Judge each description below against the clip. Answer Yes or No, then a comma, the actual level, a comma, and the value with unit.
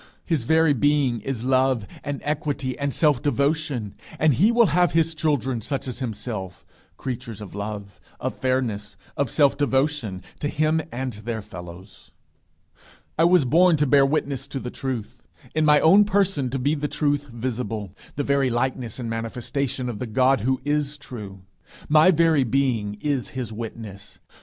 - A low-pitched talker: Yes, low, 130 Hz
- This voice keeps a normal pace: Yes, average, 165 wpm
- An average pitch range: Yes, average, 4.4 semitones